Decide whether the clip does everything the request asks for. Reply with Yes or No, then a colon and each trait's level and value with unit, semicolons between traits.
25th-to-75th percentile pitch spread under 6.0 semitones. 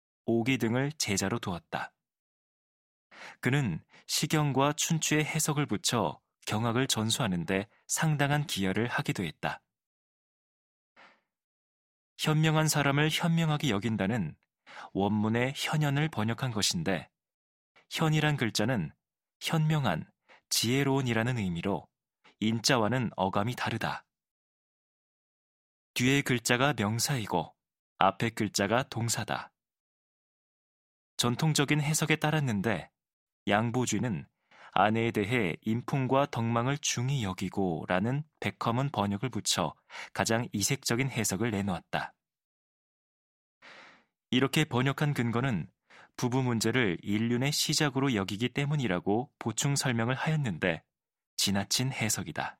Yes: average, 5.3 semitones